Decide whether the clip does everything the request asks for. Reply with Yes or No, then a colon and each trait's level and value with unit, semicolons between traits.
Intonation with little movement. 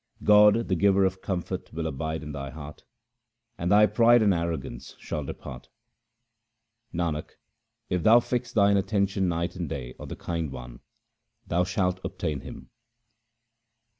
No: average, 4.3 semitones